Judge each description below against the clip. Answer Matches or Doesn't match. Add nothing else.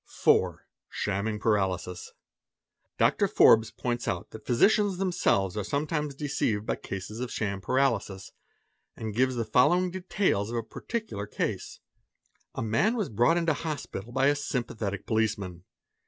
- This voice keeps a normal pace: Doesn't match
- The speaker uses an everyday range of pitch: Doesn't match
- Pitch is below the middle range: Matches